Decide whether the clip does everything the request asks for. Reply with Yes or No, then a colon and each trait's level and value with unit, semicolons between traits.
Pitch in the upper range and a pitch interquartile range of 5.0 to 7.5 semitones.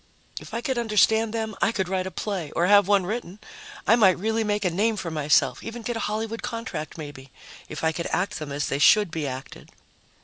Yes: high, 200 Hz; wide, 5.6 semitones